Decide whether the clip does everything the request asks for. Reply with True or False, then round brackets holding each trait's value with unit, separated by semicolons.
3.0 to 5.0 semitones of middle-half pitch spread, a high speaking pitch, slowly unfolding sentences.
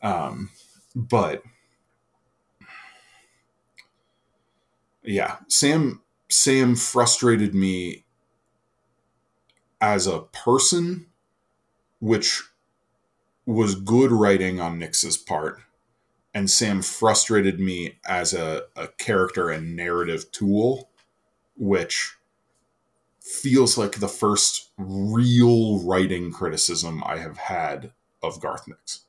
False (4.6 semitones; 105 Hz; 85 wpm)